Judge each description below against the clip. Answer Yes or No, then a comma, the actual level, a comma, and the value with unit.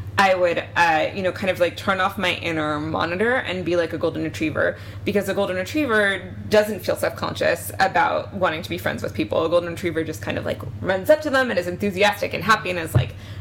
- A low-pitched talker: No, medium, 180 Hz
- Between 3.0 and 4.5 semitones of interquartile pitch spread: Yes, average, 3.8 semitones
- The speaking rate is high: Yes, fast, 235 wpm